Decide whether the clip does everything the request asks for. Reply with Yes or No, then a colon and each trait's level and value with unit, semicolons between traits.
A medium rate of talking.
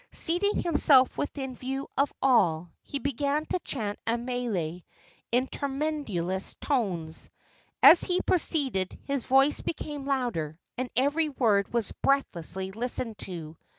No: slow, 125 wpm